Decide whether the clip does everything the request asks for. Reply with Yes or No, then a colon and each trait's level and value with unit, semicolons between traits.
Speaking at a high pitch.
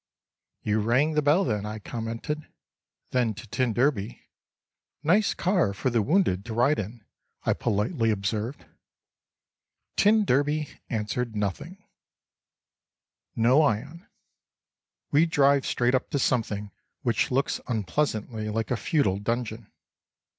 No: low, 120 Hz